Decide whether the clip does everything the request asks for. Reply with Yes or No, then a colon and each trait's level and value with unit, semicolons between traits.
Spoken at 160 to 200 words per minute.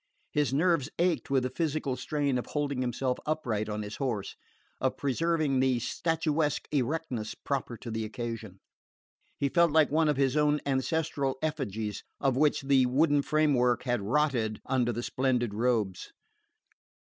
No: average, 150 wpm